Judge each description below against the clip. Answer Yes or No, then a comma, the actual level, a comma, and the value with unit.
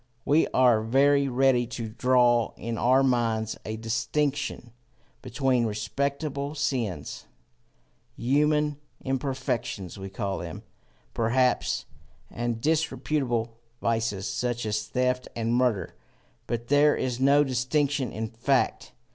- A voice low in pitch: Yes, low, 125 Hz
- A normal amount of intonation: Yes, average, 3.5 semitones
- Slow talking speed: Yes, slow, 115 wpm